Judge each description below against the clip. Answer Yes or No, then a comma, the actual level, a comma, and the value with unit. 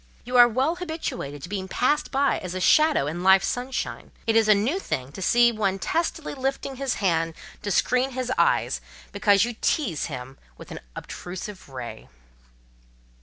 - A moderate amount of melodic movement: No, wide, 6.5 semitones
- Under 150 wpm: No, average, 170 wpm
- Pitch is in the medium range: No, high, 220 Hz